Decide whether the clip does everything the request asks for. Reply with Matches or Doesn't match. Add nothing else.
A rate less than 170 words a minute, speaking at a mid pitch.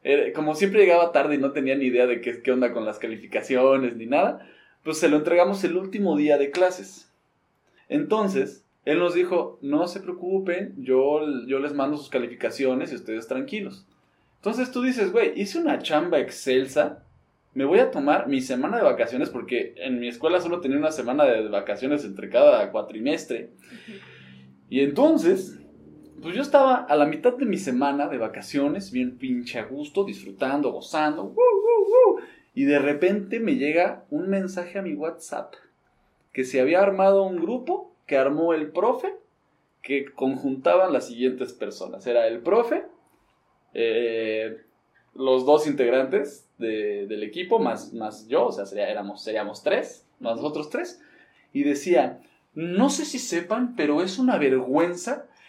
Matches